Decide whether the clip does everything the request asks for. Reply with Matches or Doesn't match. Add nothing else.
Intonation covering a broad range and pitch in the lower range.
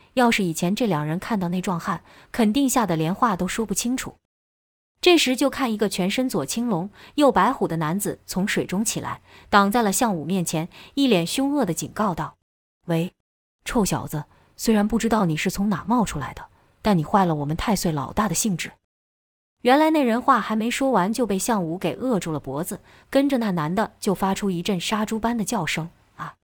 Doesn't match